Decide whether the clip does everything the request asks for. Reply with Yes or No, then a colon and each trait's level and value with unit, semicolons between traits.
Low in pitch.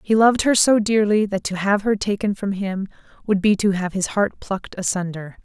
No: high, 200 Hz